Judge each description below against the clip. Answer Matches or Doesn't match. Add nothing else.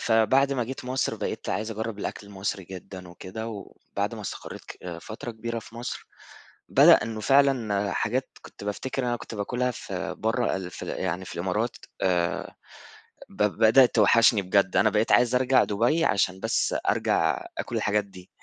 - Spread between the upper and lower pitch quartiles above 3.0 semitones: Matches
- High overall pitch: Doesn't match